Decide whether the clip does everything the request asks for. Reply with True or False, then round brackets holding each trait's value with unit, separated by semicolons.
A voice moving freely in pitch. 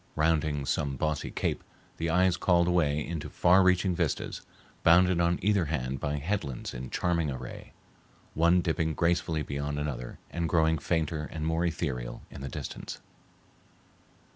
False (2.9 semitones)